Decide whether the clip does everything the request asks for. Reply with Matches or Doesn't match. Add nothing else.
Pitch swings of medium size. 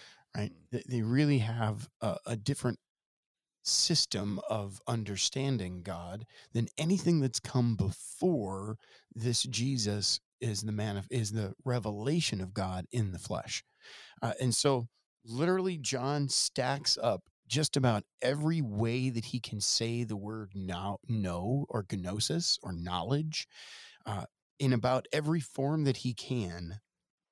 Matches